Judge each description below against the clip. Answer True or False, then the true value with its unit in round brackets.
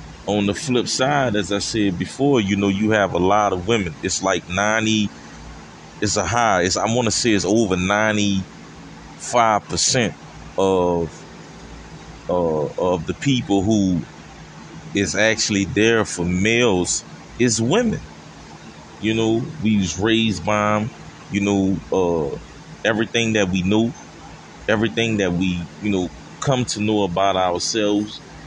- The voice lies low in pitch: True (105 Hz)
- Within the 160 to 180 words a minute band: False (140 wpm)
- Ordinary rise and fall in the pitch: True (3.0 semitones)